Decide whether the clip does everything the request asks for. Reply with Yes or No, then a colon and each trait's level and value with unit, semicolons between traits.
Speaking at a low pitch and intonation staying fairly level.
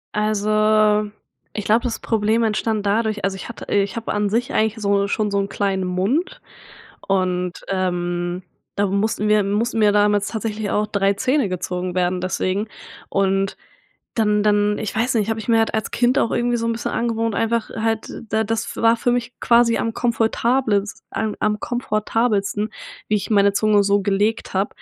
No: high, 210 Hz; narrow, 2.1 semitones